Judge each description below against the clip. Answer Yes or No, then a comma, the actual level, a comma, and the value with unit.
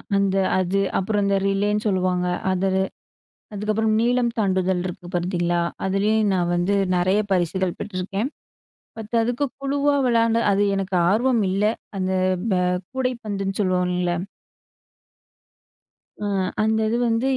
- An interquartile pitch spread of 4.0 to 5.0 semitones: No, average, 3.1 semitones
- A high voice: Yes, high, 195 Hz